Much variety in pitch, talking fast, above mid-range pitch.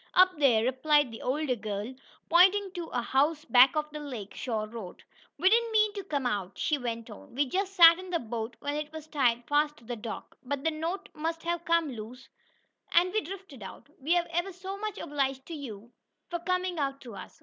Yes: wide, 6.0 semitones; fast, 215 wpm; very high, 295 Hz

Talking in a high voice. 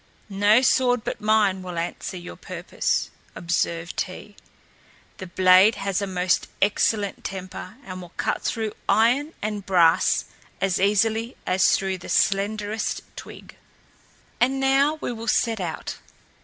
Yes: high, 200 Hz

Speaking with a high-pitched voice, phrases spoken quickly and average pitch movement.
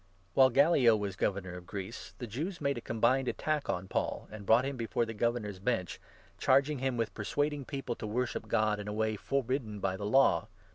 No: low, 115 Hz; fast, 220 wpm; average, 4.4 semitones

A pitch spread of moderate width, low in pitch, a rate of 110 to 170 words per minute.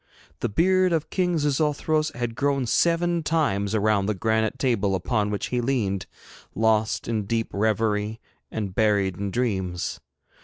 No: wide, 5.8 semitones; low, 110 Hz; average, 145 wpm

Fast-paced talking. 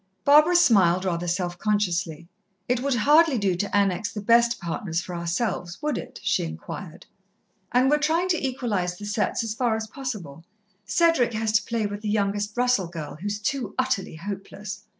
No: average, 175 wpm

